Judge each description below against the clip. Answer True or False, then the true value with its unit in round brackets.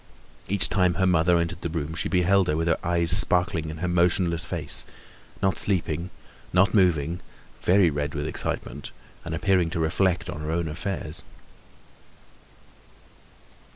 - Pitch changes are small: True (2.2 semitones)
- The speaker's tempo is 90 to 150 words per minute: True (145 wpm)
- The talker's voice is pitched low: True (85 Hz)